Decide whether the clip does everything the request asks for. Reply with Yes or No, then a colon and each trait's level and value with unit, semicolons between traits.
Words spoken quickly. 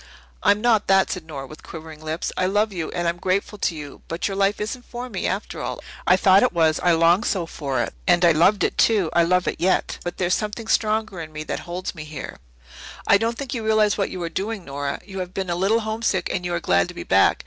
Yes: fast, 260 wpm